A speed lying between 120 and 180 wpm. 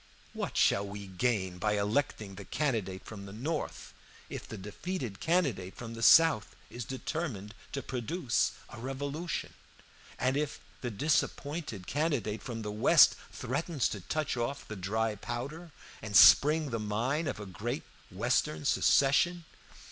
Yes: average, 145 wpm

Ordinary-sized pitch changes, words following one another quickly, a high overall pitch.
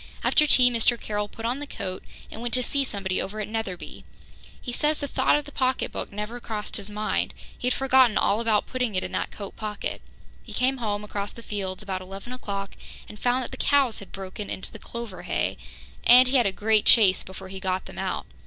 Yes: average, 3.9 semitones; fast, 225 wpm; high, 215 Hz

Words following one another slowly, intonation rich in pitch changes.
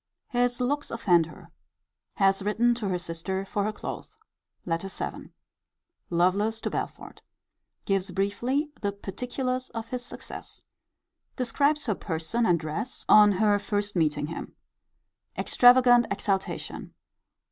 No: slow, 125 wpm; average, 4.6 semitones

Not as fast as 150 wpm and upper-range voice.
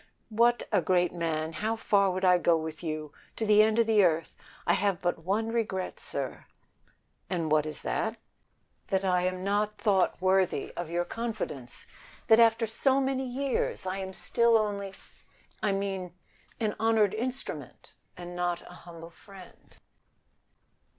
No: average, 165 wpm; high, 195 Hz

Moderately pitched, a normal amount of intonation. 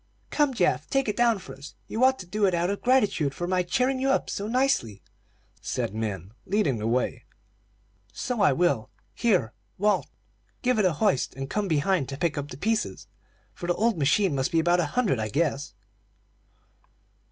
No: medium, 180 Hz; wide, 8.1 semitones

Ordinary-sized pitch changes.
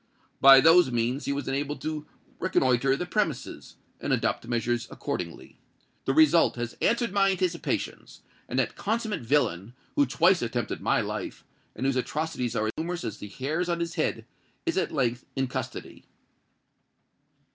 No: wide, 5.8 semitones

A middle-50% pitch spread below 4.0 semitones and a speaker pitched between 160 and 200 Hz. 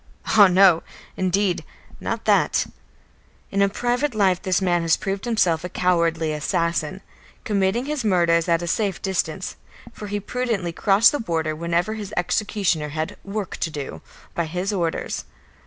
Yes: average, 3.5 semitones; medium, 185 Hz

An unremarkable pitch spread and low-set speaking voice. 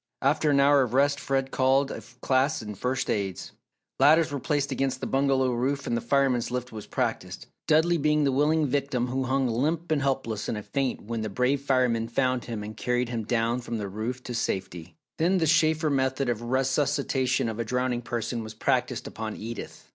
Yes: average, 3.1 semitones; low, 130 Hz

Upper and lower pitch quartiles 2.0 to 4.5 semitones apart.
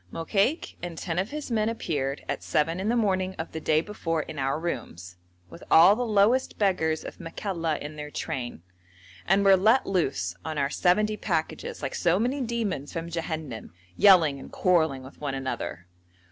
No: average, 5.3 semitones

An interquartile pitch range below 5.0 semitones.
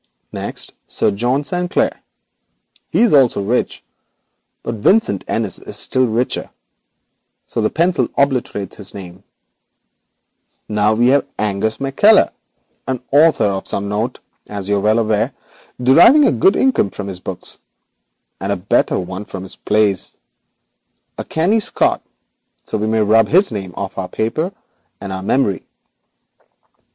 No: wide, 5.5 semitones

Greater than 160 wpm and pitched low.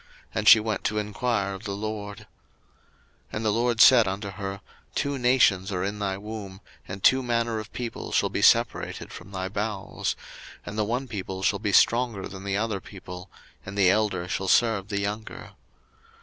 Yes: average, 185 wpm; low, 105 Hz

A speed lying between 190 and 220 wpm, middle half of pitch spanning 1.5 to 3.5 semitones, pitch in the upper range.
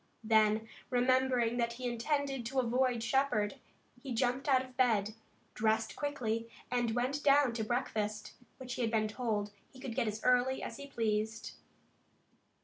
No: average, 155 wpm; average, 2.8 semitones; high, 240 Hz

